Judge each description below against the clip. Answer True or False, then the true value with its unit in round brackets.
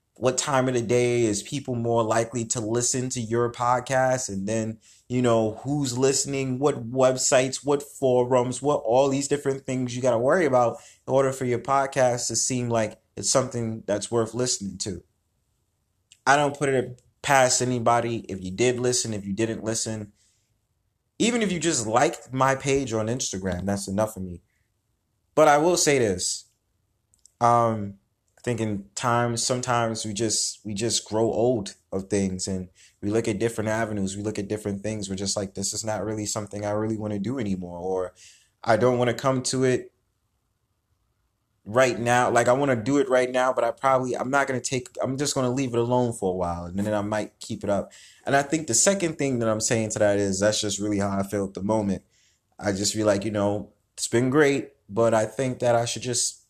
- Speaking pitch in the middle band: False (115 Hz)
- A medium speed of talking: False (210 wpm)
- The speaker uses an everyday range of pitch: True (3.5 semitones)